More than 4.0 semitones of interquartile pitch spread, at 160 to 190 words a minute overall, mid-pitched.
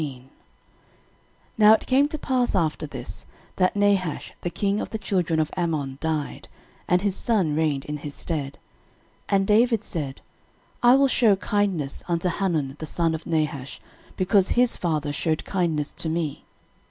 Yes: average, 5.0 semitones; average, 165 wpm; medium, 170 Hz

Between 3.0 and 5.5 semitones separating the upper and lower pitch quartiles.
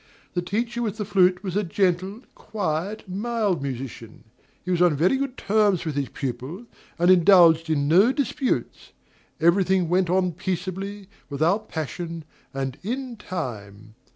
Yes: average, 4.3 semitones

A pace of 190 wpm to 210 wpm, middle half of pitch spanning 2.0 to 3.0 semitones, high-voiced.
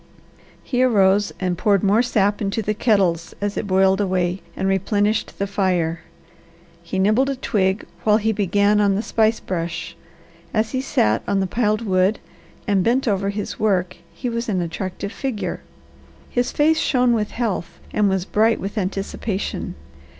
No: average, 165 wpm; narrow, 2.6 semitones; high, 200 Hz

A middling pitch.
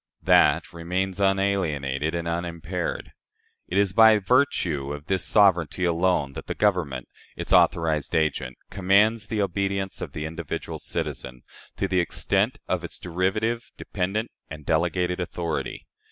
No: very low, 90 Hz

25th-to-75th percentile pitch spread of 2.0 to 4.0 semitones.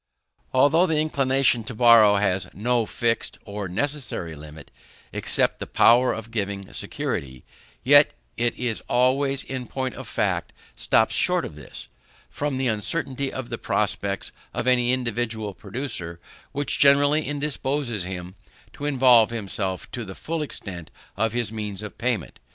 No: average, 4.7 semitones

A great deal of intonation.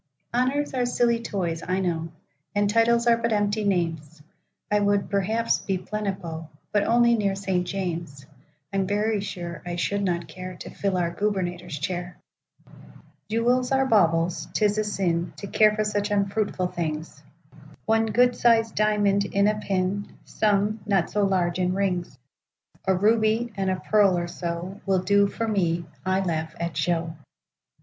No: average, 3.5 semitones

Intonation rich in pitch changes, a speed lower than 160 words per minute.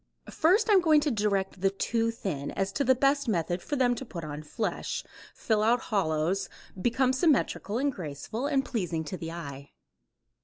No: wide, 7.3 semitones; average, 185 wpm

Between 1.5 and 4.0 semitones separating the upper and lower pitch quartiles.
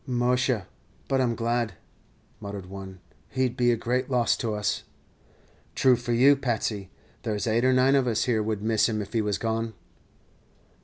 Yes: average, 2.9 semitones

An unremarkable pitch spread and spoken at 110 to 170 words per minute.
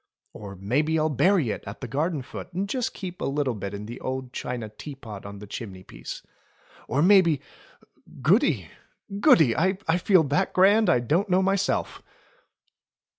No: wide, 8.0 semitones; average, 165 wpm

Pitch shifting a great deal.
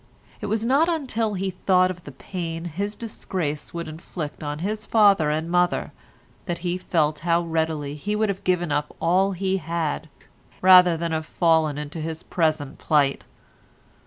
No: average, 3.4 semitones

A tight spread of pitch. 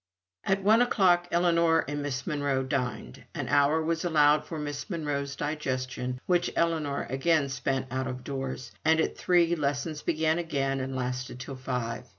No: average, 3.7 semitones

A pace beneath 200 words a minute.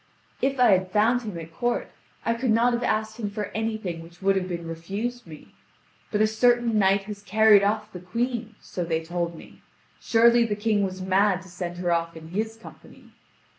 No: fast, 205 wpm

